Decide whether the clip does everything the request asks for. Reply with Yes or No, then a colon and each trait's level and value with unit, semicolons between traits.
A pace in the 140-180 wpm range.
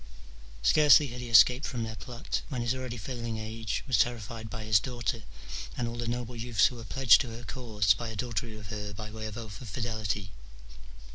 No: fast, 205 wpm